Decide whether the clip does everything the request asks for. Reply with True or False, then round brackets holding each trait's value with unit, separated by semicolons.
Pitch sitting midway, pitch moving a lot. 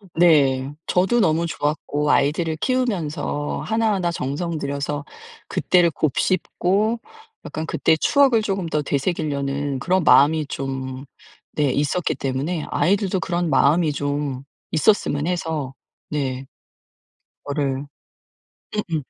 False (155 Hz; 4.0 semitones)